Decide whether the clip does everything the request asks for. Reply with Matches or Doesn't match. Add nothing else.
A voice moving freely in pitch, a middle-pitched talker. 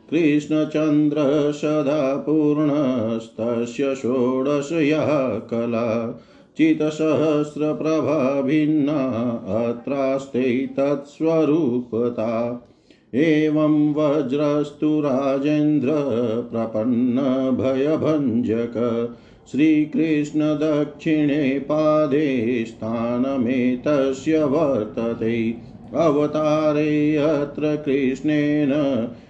Doesn't match